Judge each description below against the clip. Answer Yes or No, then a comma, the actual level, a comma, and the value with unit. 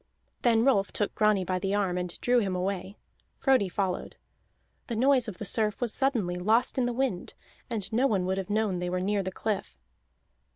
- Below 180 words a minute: No, average, 200 wpm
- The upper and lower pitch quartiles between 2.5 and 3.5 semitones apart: No, average, 3.9 semitones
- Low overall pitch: No, high, 205 Hz